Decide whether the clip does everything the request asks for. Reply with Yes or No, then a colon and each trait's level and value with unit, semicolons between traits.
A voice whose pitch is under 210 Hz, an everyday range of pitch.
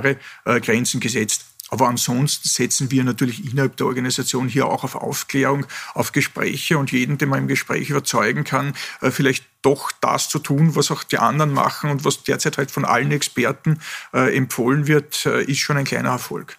No: medium, 140 Hz; narrow, 2.1 semitones